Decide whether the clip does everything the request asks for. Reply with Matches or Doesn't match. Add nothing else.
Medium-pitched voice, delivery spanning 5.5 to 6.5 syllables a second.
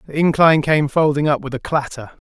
Matches